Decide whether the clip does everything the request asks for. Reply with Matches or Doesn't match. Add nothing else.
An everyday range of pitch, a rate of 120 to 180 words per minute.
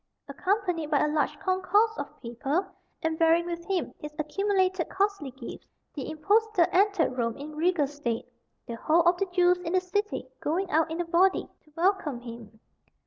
Matches